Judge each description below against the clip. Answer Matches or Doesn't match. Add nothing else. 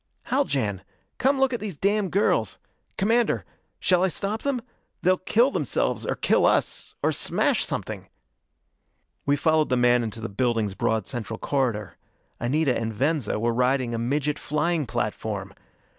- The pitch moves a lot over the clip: Matches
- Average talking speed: Matches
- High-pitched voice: Doesn't match